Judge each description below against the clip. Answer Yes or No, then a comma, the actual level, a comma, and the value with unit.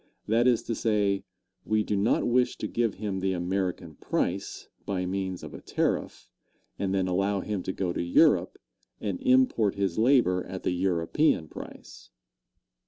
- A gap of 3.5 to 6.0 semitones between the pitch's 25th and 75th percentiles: No, average, 2.8 semitones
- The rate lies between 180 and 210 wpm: No, average, 165 wpm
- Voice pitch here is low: Yes, low, 100 Hz